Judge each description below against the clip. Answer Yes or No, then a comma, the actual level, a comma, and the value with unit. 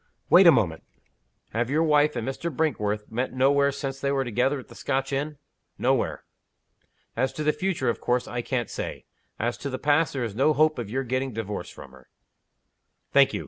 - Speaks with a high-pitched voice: No, low, 135 Hz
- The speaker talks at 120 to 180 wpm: No, average, 200 wpm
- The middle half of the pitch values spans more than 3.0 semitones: Yes, average, 3.5 semitones